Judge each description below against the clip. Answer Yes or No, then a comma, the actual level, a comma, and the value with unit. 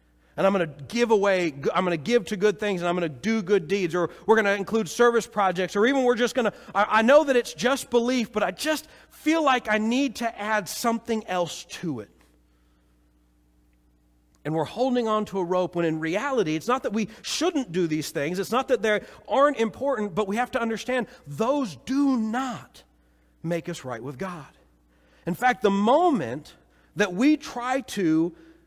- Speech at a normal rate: Yes, average, 195 wpm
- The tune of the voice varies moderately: No, wide, 6.7 semitones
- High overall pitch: Yes, high, 205 Hz